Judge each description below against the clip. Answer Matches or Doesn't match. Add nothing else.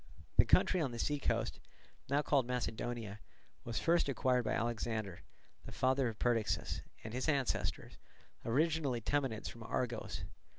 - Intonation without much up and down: Doesn't match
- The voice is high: Doesn't match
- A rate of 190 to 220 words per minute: Doesn't match